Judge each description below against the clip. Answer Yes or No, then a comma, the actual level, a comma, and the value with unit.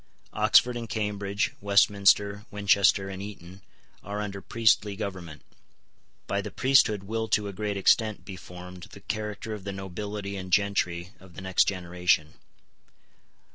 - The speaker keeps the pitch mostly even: Yes, narrow, 1.9 semitones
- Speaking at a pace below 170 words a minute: Yes, average, 140 wpm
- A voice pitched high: No, low, 100 Hz